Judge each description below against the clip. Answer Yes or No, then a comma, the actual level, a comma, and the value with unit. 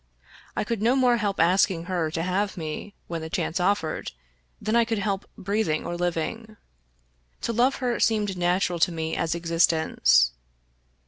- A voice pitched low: No, medium, 185 Hz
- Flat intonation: No, average, 4.4 semitones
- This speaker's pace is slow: No, average, 165 wpm